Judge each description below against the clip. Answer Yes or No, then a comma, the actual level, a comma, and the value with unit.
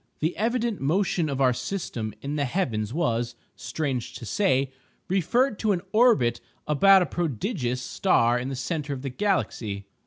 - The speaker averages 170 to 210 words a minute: No, average, 160 wpm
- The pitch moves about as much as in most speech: No, wide, 7.5 semitones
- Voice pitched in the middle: Yes, medium, 145 Hz